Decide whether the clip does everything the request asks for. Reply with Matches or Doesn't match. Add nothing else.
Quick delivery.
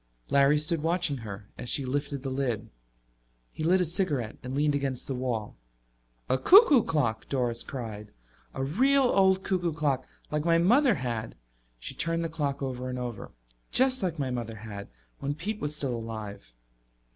Doesn't match